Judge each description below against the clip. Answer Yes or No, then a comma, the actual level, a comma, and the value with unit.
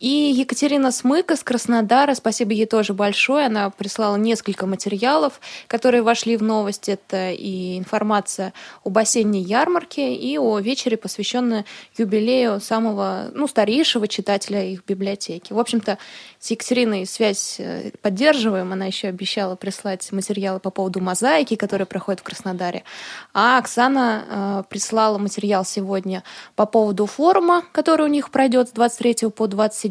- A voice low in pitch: No, high, 215 Hz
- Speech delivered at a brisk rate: No, average, 135 wpm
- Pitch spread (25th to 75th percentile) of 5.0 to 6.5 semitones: No, average, 3.7 semitones